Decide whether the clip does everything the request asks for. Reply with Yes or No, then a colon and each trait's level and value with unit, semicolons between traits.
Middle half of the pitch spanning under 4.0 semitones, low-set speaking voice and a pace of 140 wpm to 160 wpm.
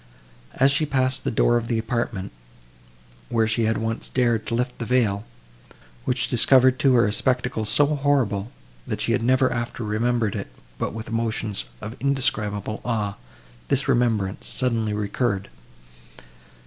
Yes: average, 2.7 semitones; low, 115 Hz; average, 150 wpm